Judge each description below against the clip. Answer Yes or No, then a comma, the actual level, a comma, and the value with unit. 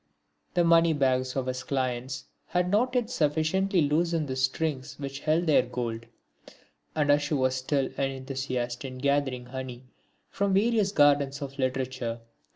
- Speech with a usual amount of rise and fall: Yes, average, 3.6 semitones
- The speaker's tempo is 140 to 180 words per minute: Yes, average, 150 wpm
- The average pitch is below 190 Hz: Yes, medium, 140 Hz